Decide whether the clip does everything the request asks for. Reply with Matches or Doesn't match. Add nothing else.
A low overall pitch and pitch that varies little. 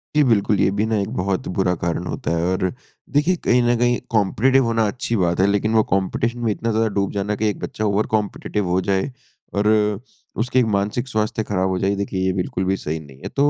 Doesn't match